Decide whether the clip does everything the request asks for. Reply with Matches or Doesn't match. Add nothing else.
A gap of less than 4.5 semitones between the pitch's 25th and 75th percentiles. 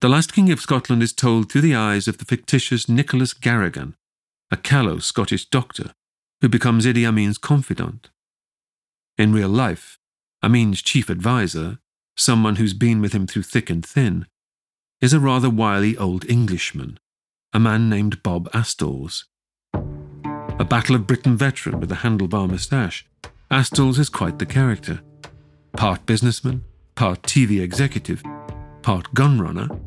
Matches